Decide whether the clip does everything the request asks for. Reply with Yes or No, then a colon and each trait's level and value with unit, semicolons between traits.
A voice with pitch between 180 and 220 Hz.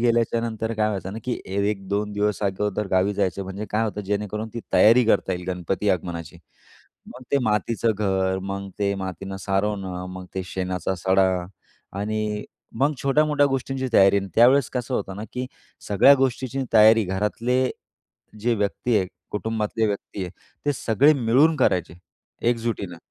No: low, 105 Hz